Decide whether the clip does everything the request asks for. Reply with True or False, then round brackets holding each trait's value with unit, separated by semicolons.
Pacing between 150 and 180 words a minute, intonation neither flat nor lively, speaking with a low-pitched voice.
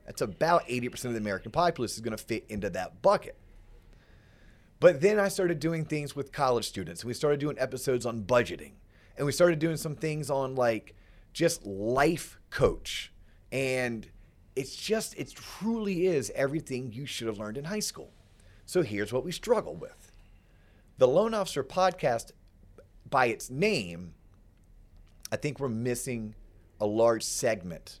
False (160 wpm; 7.0 semitones; 125 Hz)